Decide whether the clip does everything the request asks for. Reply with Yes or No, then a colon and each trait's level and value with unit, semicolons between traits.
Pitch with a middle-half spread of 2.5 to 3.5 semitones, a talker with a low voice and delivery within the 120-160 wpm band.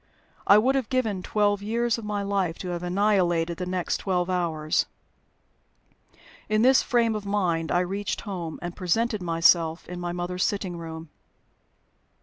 No: average, 3.2 semitones; medium, 185 Hz; average, 155 wpm